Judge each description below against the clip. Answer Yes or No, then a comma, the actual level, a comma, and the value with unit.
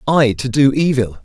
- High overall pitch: No, low, 130 Hz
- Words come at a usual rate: Yes, average, 195 wpm